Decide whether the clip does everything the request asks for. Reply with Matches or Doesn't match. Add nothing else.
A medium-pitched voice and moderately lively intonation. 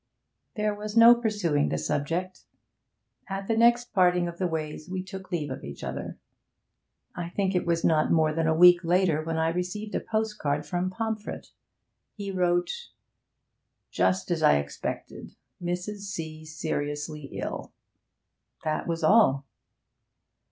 Matches